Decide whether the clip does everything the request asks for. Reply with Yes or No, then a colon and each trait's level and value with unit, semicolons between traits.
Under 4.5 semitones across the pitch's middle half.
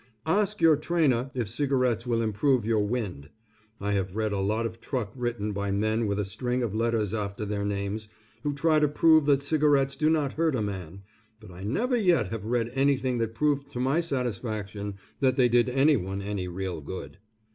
No: average, 5.2 semitones